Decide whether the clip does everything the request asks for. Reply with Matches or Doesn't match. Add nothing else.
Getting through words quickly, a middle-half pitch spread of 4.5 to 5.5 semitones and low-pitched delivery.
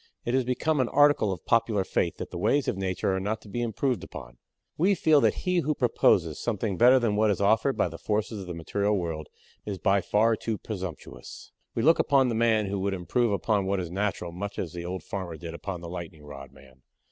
Matches